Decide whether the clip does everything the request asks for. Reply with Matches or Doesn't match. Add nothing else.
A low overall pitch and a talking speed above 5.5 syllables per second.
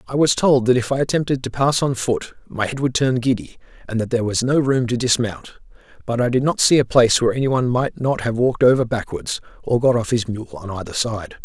Matches